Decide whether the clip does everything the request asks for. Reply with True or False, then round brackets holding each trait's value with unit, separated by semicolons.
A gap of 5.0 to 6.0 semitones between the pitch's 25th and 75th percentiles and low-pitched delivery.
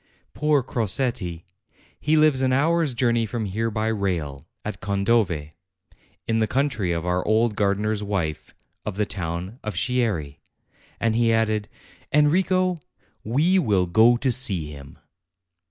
True (5.4 semitones; 110 Hz)